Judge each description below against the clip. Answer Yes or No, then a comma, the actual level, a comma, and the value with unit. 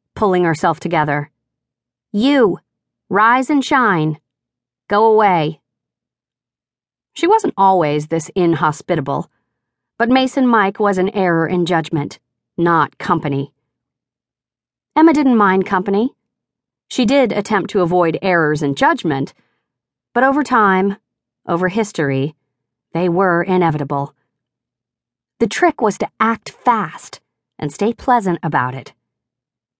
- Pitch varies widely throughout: Yes, wide, 7.3 semitones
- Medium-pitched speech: Yes, medium, 175 Hz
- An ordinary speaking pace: No, slow, 110 wpm